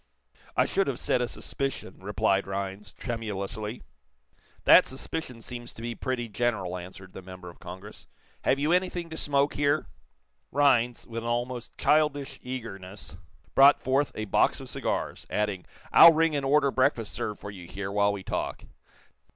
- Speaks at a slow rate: No, average, 160 wpm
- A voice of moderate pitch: No, low, 115 Hz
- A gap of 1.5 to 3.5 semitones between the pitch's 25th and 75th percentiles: No, wide, 5.6 semitones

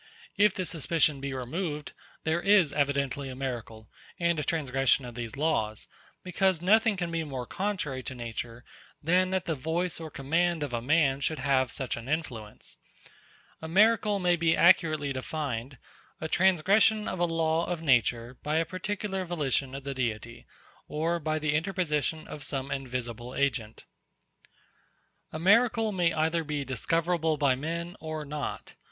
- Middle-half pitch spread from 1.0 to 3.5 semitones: No, average, 4.5 semitones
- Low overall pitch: No, medium, 155 Hz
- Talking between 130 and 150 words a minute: No, average, 160 wpm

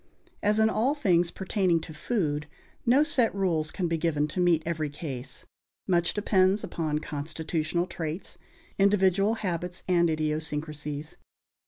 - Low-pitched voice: No, medium, 170 Hz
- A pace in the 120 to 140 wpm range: Yes, slow, 135 wpm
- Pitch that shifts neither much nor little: Yes, average, 3.9 semitones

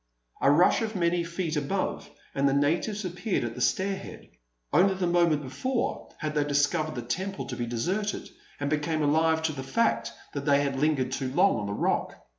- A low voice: No, medium, 155 Hz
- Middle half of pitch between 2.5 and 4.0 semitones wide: No, average, 4.5 semitones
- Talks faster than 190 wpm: Yes, average, 200 wpm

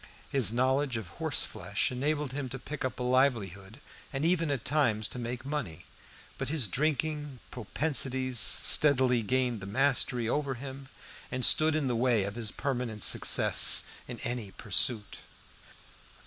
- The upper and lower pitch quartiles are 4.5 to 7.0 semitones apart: No, average, 3.4 semitones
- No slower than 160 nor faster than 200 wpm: No, average, 150 wpm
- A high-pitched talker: No, low, 130 Hz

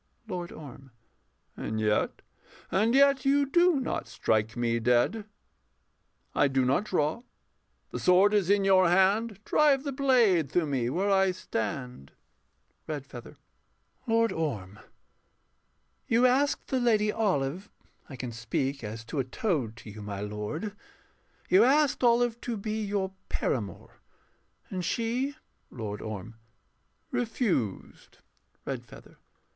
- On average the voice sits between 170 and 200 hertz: Yes, medium, 185 Hz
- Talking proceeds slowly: Yes, slow, 125 wpm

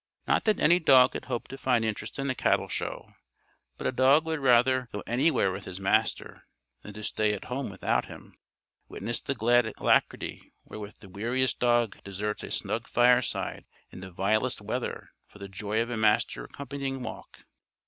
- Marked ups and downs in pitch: No, average, 3.8 semitones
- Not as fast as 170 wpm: No, average, 180 wpm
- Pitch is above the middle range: No, low, 120 Hz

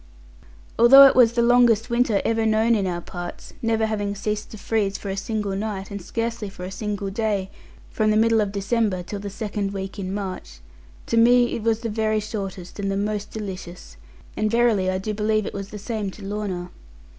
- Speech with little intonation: Yes, narrow, 2.3 semitones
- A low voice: No, high, 210 Hz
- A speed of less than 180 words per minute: No, fast, 205 wpm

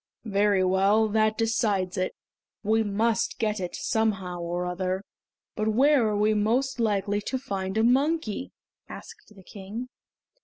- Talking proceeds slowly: No, average, 145 wpm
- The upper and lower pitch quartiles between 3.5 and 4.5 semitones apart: No, average, 2.9 semitones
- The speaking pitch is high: Yes, high, 215 Hz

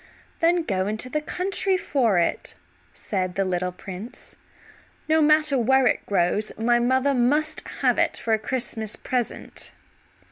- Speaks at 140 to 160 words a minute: Yes, average, 145 wpm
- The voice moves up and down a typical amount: No, wide, 6.6 semitones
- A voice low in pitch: No, high, 240 Hz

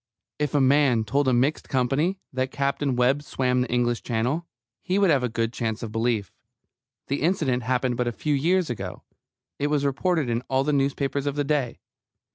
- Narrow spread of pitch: No, average, 3.1 semitones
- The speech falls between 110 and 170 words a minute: No, average, 195 wpm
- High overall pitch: No, low, 135 Hz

